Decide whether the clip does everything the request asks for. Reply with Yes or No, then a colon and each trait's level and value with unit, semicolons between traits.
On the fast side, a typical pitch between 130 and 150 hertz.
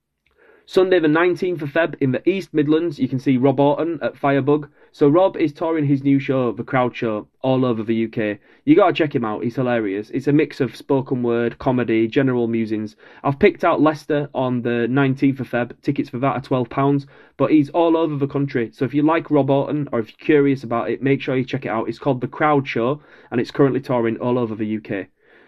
Yes: fast, 230 wpm; low, 135 Hz